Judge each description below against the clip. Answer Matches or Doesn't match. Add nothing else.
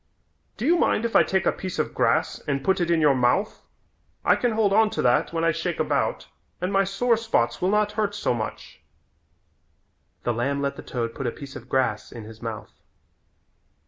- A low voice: Doesn't match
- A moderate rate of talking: Doesn't match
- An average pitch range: Doesn't match